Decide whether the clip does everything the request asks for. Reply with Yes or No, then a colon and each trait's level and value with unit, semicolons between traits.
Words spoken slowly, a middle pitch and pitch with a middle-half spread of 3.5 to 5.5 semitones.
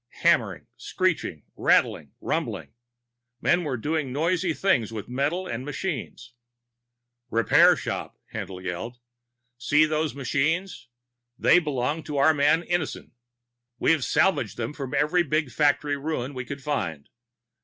Yes: slow, 125 wpm; medium, 145 Hz; average, 4.4 semitones